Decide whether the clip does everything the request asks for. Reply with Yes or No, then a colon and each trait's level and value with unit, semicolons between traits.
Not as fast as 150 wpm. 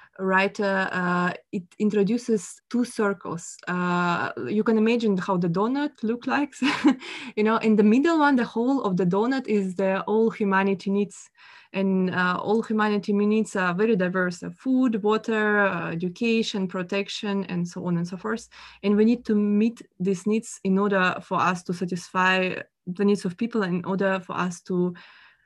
No: average, 170 wpm